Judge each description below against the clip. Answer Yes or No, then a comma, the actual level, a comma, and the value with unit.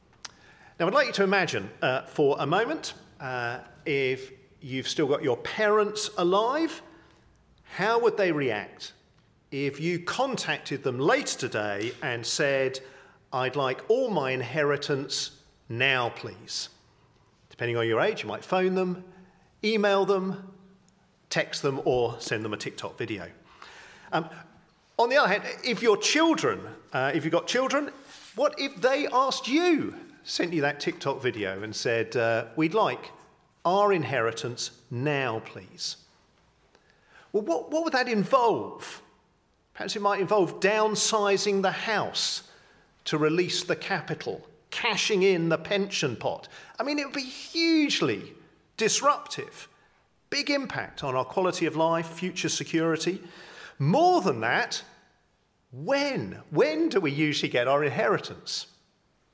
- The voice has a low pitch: No, medium, 180 Hz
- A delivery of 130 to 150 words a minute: Yes, average, 140 wpm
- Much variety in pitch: Yes, wide, 8.2 semitones